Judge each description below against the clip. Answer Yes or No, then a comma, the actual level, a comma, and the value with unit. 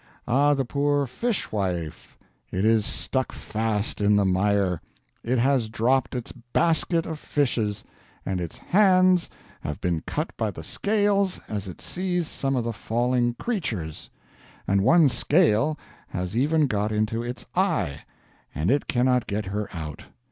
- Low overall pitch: Yes, low, 120 Hz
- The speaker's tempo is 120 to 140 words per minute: No, average, 150 wpm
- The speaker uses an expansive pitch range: Yes, wide, 6.2 semitones